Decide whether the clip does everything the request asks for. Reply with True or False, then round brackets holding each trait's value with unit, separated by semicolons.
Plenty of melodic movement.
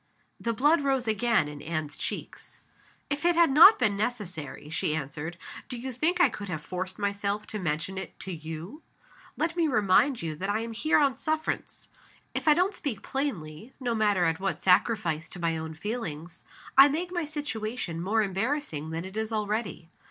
True (8.0 semitones)